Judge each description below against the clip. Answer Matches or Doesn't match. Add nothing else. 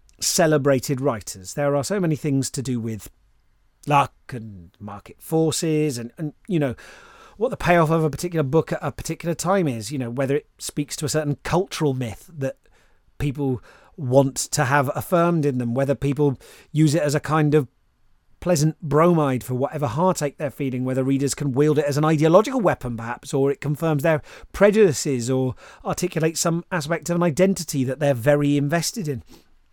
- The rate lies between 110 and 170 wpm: Doesn't match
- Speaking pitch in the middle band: Matches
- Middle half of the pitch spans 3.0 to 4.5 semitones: Matches